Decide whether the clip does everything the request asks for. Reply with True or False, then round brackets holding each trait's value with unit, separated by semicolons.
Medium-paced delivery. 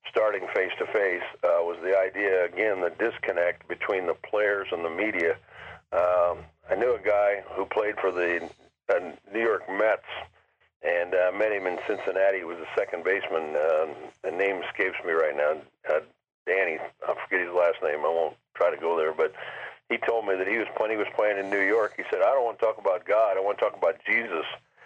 False (215 wpm)